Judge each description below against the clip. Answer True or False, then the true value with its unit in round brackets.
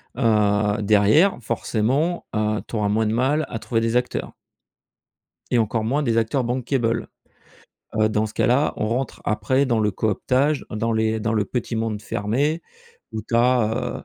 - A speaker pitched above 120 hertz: False (115 Hz)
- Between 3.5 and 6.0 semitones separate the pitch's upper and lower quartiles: False (2.9 semitones)